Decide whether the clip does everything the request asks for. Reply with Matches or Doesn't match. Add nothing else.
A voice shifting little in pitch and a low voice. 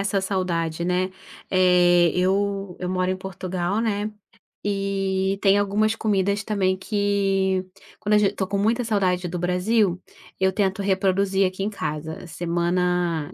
Doesn't match